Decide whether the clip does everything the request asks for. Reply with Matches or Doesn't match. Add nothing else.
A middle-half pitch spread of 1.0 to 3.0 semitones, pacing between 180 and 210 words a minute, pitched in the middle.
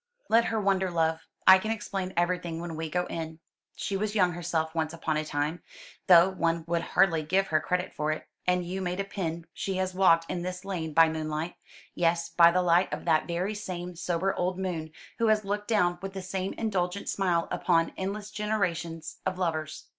Matches